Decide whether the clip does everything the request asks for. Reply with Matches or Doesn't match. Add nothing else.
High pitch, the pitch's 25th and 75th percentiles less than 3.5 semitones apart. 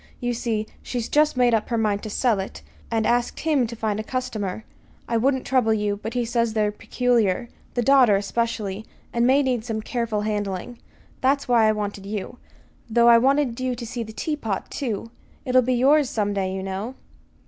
Matches